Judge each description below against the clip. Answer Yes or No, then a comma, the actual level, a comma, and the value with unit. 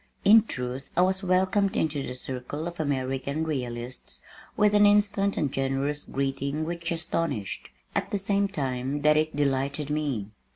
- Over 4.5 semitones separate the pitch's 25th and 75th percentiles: Yes, wide, 5.4 semitones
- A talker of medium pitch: Yes, medium, 150 Hz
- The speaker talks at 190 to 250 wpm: No, average, 155 wpm